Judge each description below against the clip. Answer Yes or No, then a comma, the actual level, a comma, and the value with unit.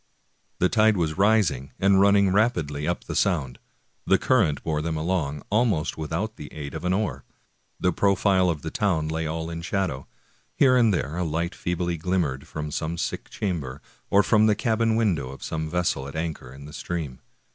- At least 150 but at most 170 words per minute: No, average, 190 wpm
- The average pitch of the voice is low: Yes, very low, 85 Hz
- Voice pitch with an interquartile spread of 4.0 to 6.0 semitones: Yes, average, 4.4 semitones